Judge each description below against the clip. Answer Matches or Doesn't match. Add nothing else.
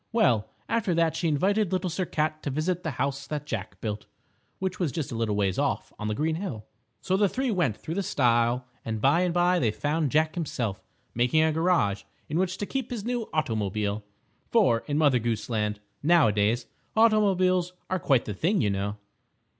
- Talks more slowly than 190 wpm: Doesn't match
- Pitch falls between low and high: Matches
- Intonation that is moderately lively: Doesn't match